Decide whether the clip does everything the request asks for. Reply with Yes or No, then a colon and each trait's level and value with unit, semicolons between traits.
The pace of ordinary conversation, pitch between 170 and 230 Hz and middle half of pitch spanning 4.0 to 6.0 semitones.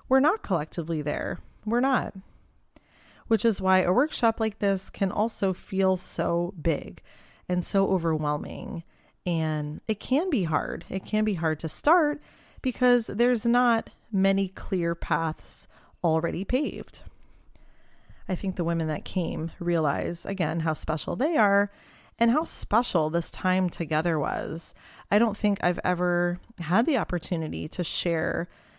Yes: average, 145 wpm; medium, 185 Hz; average, 4.6 semitones